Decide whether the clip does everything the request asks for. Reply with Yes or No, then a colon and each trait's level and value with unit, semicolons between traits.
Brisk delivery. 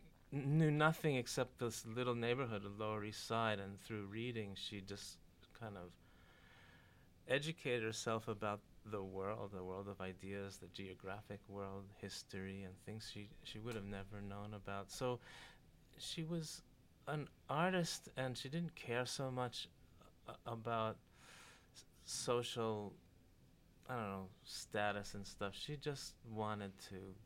No: slow, 135 wpm